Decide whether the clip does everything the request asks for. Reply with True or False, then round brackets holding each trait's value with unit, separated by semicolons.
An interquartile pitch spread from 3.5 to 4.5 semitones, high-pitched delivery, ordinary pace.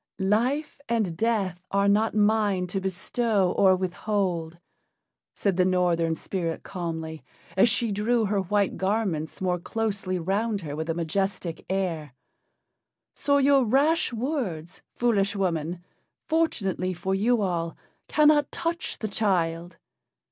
False (4.2 semitones; 195 Hz; 130 wpm)